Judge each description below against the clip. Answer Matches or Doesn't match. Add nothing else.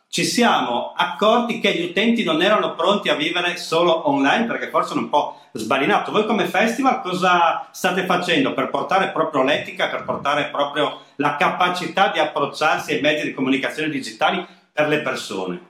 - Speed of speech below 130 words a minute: Doesn't match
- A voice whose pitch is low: Doesn't match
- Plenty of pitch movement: Doesn't match